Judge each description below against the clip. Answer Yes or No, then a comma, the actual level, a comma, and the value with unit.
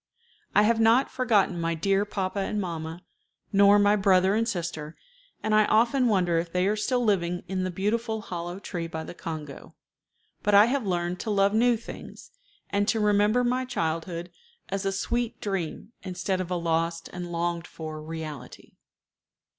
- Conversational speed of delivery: Yes, average, 170 wpm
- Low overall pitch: No, high, 190 Hz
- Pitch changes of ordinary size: Yes, average, 3.8 semitones